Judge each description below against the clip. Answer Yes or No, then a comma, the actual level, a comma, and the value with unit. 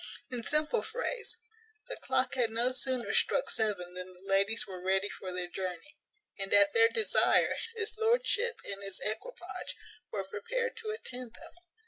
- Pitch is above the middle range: Yes, high, 225 Hz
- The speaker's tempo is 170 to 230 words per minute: No, average, 160 wpm